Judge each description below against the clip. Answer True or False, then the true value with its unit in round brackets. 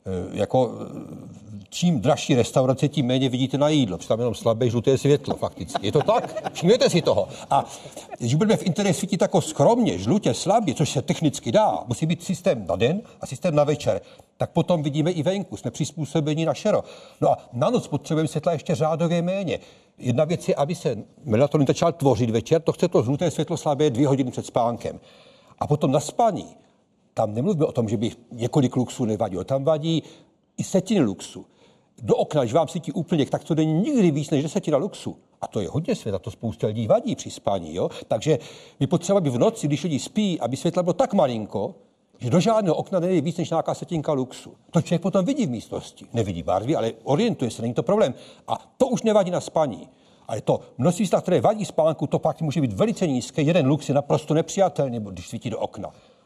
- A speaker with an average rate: False (205 wpm)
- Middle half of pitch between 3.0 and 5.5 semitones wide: True (5.2 semitones)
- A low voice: False (155 Hz)